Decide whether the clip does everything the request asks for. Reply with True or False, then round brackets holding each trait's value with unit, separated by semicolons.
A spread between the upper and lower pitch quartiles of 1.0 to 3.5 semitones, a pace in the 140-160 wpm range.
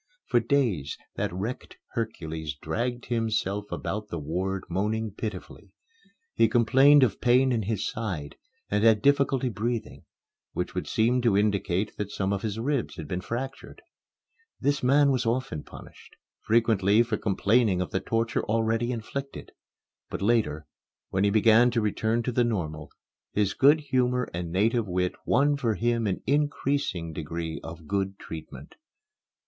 False (4.2 semitones; 155 wpm)